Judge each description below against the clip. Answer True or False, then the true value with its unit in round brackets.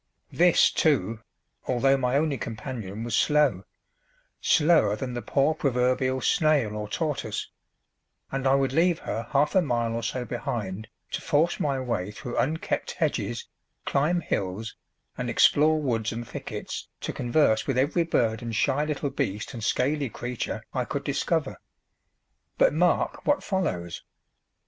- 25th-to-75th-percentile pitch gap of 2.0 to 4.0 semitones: False (4.6 semitones)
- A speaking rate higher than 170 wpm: False (145 wpm)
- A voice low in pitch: True (130 Hz)